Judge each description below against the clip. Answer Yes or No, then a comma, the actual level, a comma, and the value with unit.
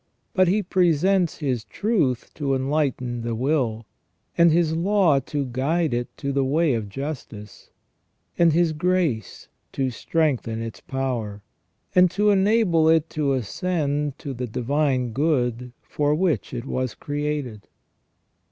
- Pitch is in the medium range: Yes, medium, 145 Hz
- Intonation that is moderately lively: Yes, average, 5.0 semitones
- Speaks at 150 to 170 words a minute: No, slow, 135 wpm